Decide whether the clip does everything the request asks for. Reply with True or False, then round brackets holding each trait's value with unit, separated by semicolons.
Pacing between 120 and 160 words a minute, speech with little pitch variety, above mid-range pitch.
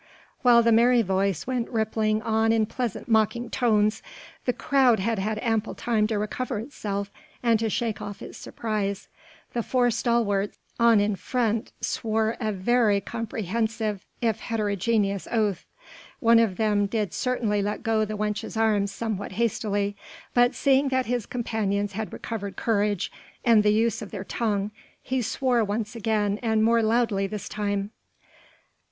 True (155 wpm; 2.2 semitones; 220 Hz)